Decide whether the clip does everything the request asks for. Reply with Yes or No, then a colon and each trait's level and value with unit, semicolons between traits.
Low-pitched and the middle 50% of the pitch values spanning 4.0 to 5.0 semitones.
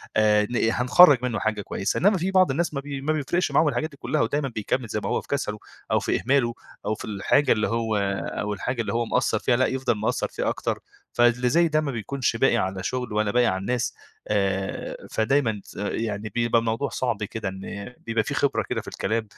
Yes: low, 120 Hz; average, 4.3 semitones